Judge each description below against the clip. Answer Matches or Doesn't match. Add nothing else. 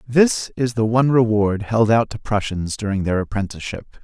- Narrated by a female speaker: Doesn't match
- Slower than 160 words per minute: Doesn't match